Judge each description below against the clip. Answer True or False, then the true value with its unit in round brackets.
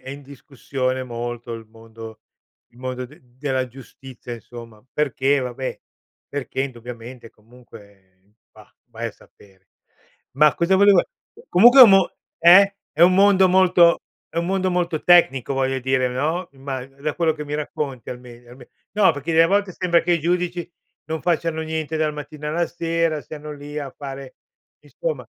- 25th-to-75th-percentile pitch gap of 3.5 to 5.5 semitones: True (5.2 semitones)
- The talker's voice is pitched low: False (145 Hz)